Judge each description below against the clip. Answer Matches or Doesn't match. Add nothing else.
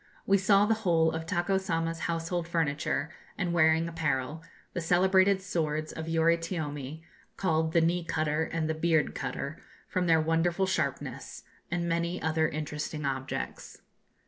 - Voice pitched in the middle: Matches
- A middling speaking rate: Matches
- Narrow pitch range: Matches